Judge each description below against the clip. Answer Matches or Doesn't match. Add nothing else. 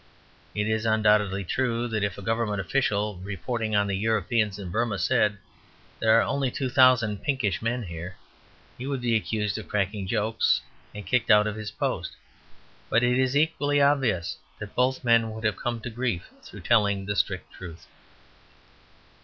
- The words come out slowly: Doesn't match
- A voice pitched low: Matches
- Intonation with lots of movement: Doesn't match